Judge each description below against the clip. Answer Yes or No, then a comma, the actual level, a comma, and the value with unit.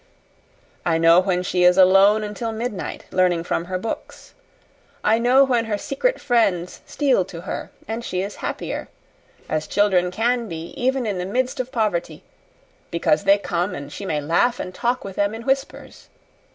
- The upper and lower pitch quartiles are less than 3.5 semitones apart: No, average, 4.9 semitones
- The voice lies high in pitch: Yes, high, 200 Hz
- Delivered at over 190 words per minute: No, average, 175 wpm